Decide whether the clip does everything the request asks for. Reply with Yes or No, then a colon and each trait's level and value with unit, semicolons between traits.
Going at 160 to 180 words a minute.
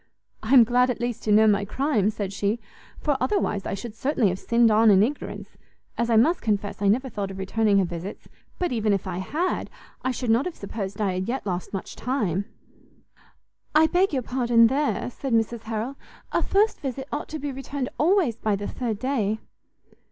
No: fast, 205 wpm